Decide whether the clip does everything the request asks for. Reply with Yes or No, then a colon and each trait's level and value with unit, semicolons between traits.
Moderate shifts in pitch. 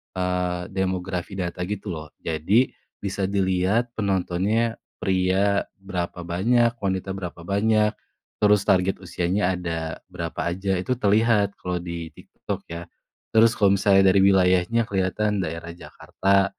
No: narrow, 2.3 semitones